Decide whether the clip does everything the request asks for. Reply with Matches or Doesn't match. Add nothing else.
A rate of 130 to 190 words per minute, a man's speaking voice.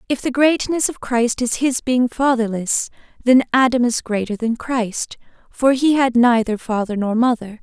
Doesn't match